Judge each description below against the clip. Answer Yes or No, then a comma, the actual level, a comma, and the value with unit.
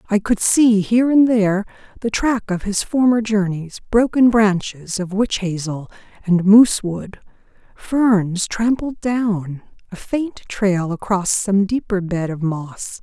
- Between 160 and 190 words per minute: No, average, 145 wpm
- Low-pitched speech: No, high, 205 Hz